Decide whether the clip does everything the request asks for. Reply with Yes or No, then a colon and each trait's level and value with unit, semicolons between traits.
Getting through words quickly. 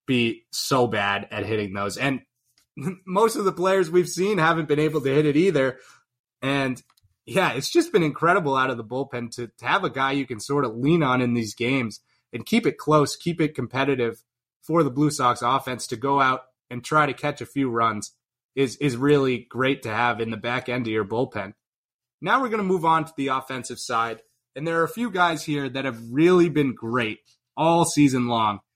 Yes: fast, 215 wpm